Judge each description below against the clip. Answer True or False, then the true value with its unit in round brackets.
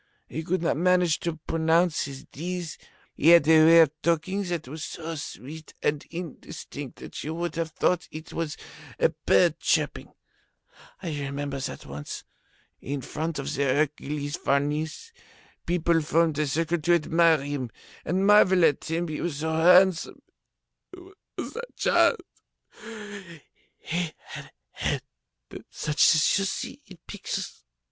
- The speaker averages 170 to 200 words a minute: False (145 wpm)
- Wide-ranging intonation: False (2.6 semitones)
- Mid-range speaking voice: True (160 Hz)